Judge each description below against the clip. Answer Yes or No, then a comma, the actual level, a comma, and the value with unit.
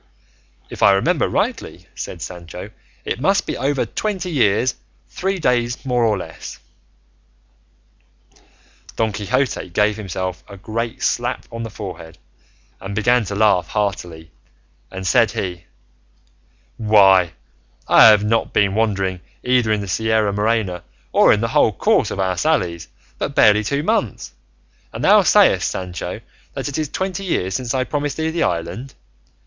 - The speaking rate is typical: Yes, average, 150 wpm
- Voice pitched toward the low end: Yes, low, 105 Hz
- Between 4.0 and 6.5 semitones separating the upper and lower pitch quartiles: Yes, average, 4.9 semitones